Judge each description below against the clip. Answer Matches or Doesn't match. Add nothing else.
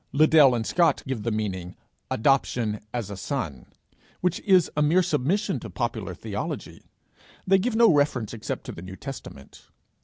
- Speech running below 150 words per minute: Doesn't match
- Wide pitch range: Matches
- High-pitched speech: Doesn't match